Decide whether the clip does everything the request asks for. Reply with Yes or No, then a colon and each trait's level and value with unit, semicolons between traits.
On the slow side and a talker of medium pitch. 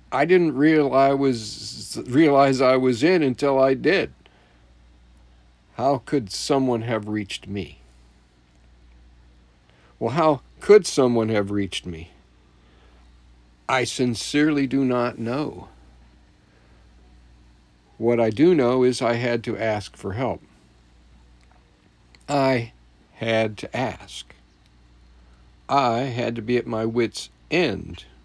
No: slow, 115 wpm; very low, 95 Hz